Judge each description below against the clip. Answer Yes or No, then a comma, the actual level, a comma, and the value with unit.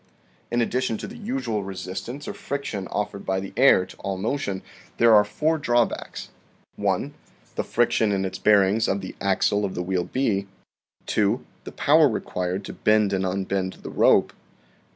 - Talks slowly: No, average, 170 wpm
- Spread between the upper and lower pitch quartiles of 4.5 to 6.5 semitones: No, average, 3.9 semitones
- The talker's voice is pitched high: No, low, 100 Hz